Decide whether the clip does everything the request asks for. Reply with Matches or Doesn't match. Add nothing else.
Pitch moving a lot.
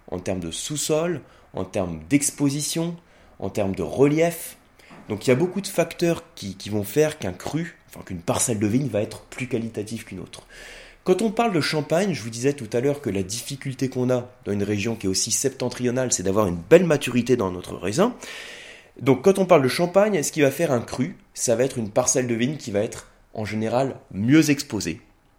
Matches